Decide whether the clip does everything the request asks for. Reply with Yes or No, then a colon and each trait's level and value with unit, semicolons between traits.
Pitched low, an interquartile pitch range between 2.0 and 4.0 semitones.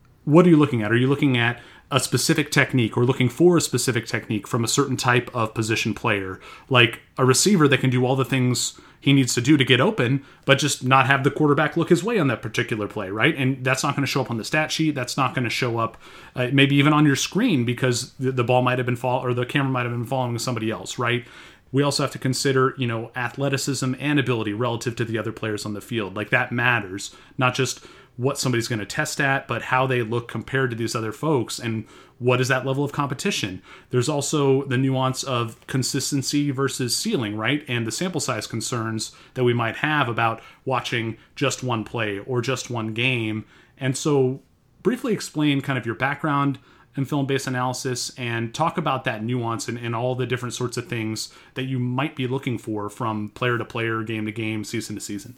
Yes: low, 125 Hz; average, 2.9 semitones